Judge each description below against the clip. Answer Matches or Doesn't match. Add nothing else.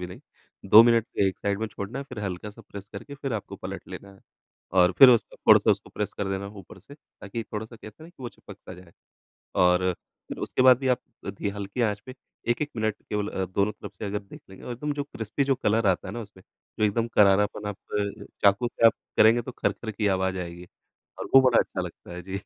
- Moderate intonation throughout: Matches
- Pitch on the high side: Doesn't match